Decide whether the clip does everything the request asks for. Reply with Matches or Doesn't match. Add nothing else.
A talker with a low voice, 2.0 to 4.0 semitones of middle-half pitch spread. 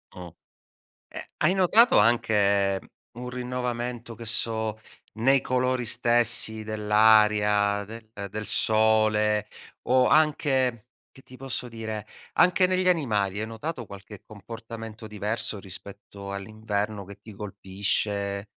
Matches